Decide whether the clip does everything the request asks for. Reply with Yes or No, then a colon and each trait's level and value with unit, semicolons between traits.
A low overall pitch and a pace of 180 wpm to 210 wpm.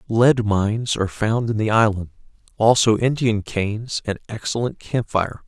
No: low, 110 Hz; average, 145 wpm